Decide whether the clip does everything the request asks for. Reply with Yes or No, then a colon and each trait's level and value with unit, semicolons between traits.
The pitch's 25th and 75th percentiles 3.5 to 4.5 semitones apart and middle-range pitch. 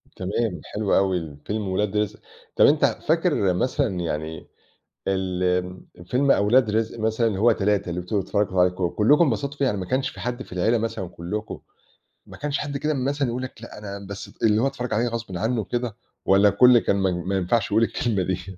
No: average, 4.2 semitones; low, 105 Hz